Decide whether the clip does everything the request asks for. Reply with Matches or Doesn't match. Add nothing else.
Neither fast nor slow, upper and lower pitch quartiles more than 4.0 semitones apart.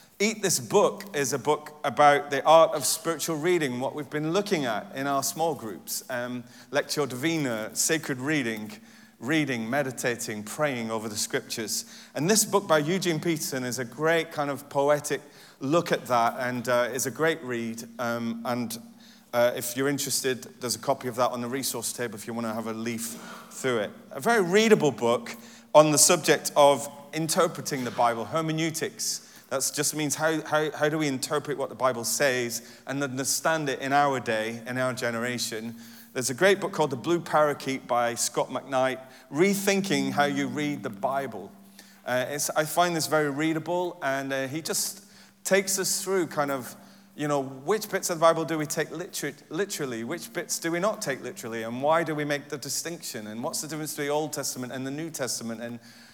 Matches